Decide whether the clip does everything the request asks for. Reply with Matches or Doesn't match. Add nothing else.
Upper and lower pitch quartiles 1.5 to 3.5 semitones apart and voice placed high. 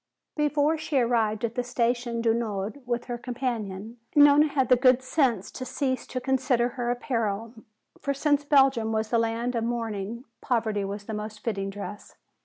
Matches